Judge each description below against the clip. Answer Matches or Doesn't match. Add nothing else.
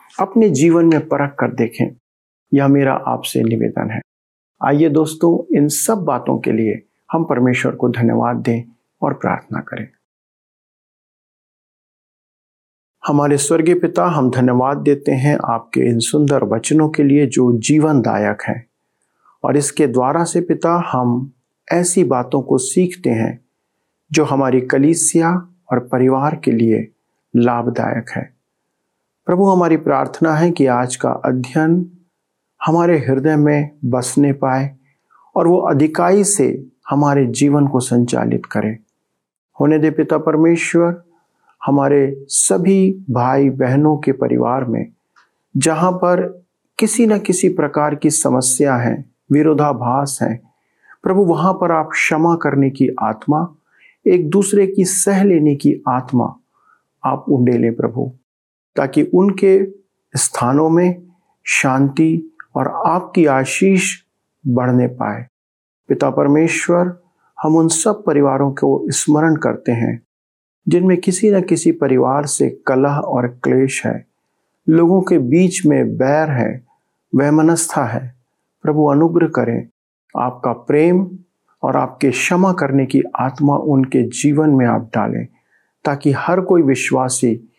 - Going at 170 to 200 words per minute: Doesn't match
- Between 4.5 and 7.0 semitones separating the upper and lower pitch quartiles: Matches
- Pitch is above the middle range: Doesn't match